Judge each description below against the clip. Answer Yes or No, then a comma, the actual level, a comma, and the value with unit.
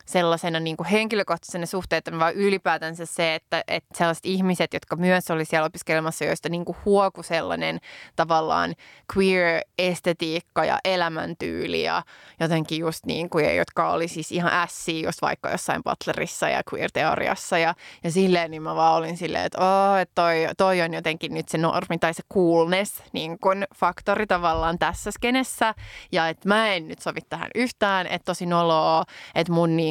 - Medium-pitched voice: Yes, medium, 170 Hz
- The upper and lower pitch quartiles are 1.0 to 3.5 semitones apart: Yes, narrow, 2.4 semitones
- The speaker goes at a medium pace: No, fast, 160 wpm